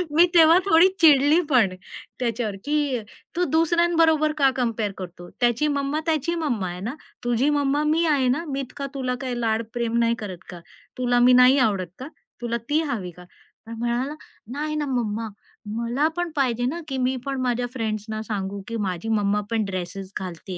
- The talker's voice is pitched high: Yes, very high, 250 Hz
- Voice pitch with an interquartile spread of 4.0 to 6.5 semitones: Yes, average, 5.3 semitones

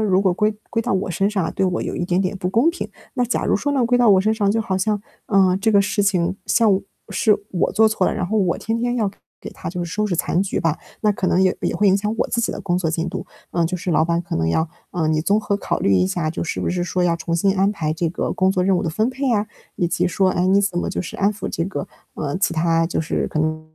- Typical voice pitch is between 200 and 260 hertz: No, high, 190 Hz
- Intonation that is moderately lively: Yes, average, 3.6 semitones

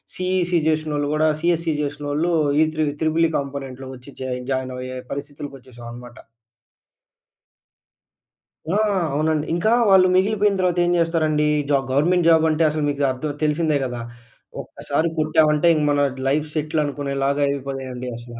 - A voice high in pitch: No, medium, 150 Hz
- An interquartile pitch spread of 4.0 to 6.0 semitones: No, average, 2.9 semitones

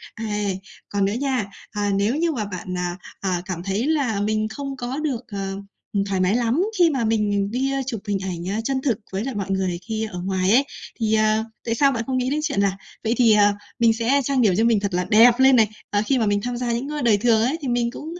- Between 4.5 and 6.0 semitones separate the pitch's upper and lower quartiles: No, average, 4.1 semitones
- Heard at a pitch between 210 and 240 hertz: Yes, high, 220 Hz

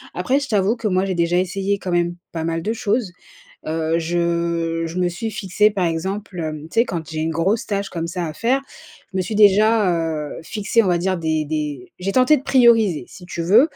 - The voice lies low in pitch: No, medium, 185 Hz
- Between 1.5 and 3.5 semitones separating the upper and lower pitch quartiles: No, average, 4.2 semitones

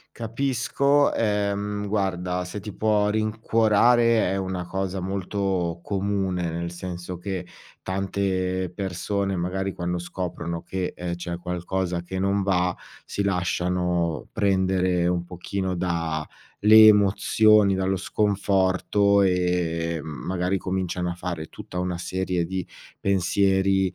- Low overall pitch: Yes, very low, 95 Hz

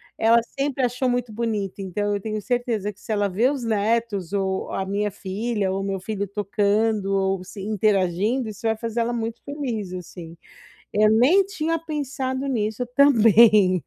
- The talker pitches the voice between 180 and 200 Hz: No, high, 215 Hz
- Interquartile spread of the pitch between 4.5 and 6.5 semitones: No, average, 3.5 semitones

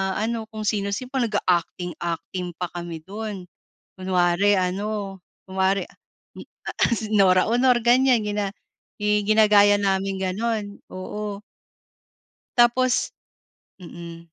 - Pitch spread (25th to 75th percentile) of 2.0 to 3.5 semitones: Yes, average, 2.7 semitones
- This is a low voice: No, high, 205 Hz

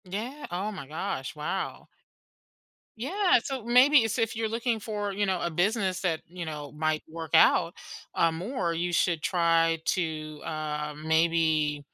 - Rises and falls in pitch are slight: No, wide, 5.4 semitones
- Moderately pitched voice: Yes, medium, 170 Hz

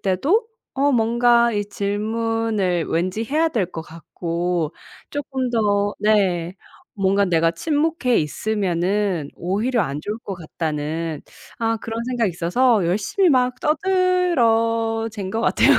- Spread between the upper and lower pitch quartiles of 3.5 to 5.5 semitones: Yes, average, 5.2 semitones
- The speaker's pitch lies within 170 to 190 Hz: No, high, 215 Hz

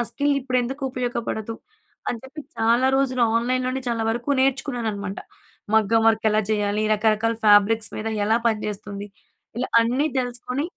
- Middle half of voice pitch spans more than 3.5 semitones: No, average, 2.8 semitones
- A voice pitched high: Yes, high, 230 Hz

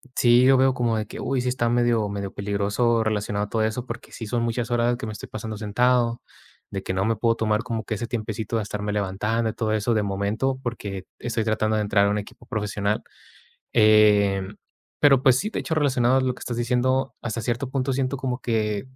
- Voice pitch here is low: Yes, low, 115 Hz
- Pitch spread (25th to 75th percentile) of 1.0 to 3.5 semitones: Yes, average, 2.8 semitones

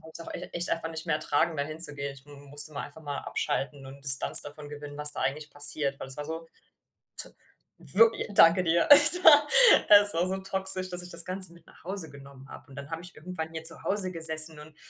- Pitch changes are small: No, average, 3.6 semitones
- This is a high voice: No, medium, 160 Hz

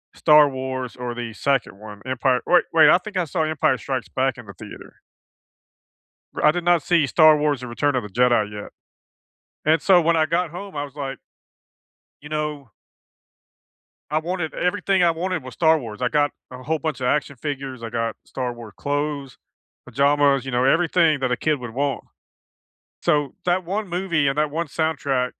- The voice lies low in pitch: No, medium, 145 Hz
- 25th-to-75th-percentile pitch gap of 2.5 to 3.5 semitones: No, average, 4.0 semitones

